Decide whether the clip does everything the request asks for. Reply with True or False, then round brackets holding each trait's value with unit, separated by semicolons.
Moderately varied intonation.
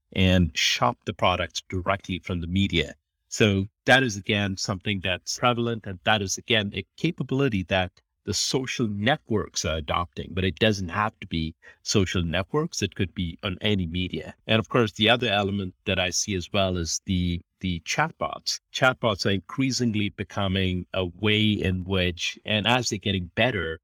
True (3.1 semitones)